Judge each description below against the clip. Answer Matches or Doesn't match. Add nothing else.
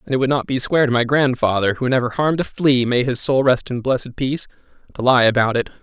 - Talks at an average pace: Doesn't match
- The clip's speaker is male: Matches